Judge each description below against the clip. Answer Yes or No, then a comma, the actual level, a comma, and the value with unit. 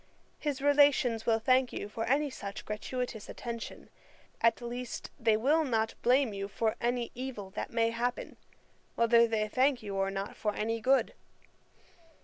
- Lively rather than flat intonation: No, average, 2.8 semitones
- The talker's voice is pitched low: No, high, 235 Hz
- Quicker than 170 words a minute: No, average, 155 wpm